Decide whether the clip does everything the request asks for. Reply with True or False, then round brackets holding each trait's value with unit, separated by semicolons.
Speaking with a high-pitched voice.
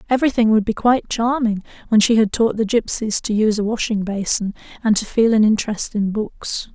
True (220 Hz)